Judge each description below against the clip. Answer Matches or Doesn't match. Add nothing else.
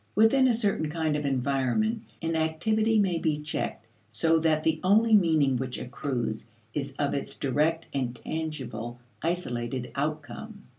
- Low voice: Doesn't match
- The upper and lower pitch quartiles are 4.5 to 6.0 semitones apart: Matches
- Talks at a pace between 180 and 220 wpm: Doesn't match